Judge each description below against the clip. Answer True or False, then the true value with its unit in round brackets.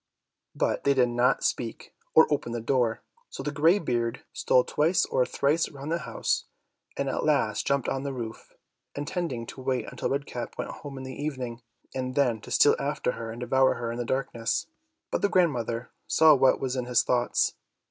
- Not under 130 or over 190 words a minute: False (200 wpm)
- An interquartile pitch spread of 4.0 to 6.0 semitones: False (2.9 semitones)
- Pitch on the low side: True (130 Hz)